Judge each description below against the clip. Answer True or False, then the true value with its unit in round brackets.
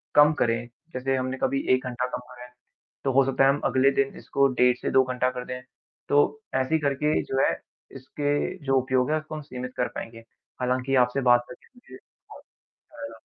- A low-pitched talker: True (130 Hz)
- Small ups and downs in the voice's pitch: True (1.8 semitones)